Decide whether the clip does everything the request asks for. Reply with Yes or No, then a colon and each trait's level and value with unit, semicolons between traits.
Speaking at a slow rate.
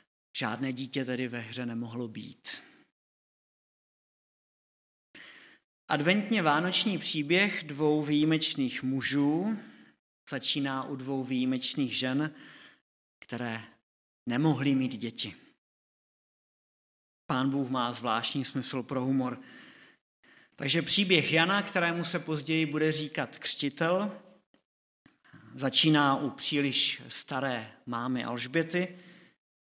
Yes: slow, 90 wpm